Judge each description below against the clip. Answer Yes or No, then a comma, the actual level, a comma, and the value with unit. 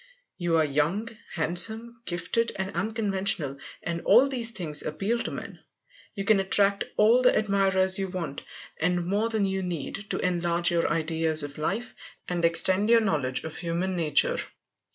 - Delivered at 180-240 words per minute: No, average, 160 wpm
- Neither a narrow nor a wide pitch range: Yes, average, 3.9 semitones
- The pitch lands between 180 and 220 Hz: Yes, medium, 185 Hz